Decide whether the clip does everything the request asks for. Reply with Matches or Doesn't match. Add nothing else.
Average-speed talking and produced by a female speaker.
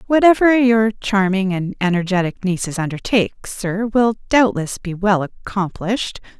Doesn't match